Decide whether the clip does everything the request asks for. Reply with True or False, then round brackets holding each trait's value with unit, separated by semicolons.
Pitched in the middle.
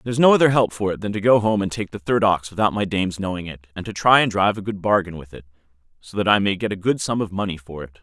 False (100 Hz)